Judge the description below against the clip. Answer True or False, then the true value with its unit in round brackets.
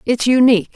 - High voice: True (240 Hz)